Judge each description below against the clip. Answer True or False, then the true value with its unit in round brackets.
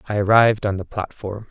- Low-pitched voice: True (105 Hz)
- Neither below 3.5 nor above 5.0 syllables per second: False (6.0 syllables/s)